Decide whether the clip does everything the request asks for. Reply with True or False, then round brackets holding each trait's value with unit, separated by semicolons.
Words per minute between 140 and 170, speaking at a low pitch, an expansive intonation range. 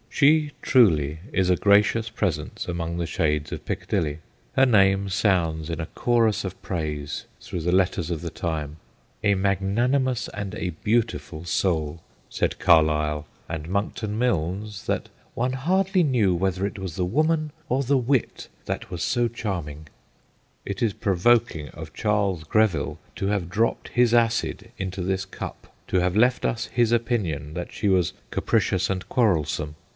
True (160 wpm; 95 Hz; 5.8 semitones)